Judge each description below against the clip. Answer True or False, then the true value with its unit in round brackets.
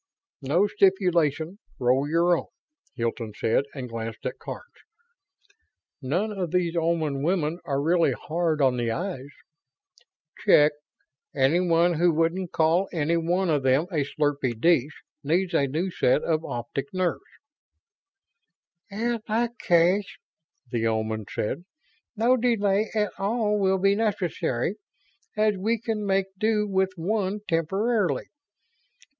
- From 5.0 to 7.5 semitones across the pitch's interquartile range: True (5.5 semitones)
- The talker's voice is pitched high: False (170 Hz)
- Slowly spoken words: True (125 wpm)